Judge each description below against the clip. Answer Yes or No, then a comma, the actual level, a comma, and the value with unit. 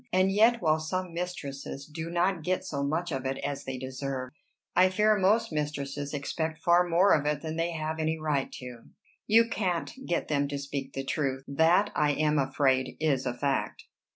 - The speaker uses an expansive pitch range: No, average, 3.9 semitones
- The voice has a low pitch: No, medium, 155 Hz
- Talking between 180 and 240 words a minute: Yes, average, 190 wpm